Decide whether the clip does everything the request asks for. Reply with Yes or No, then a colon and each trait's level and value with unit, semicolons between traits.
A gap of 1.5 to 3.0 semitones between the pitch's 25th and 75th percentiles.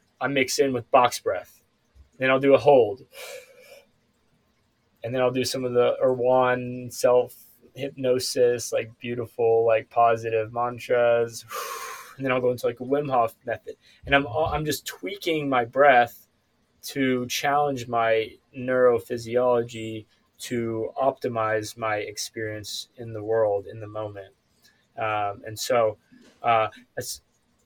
Yes: narrow, 2.6 semitones